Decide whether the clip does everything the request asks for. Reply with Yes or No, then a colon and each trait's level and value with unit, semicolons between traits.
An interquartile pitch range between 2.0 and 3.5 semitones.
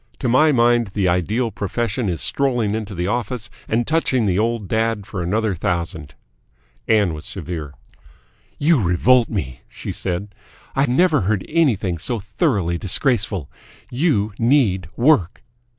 No: average, 5.0 semitones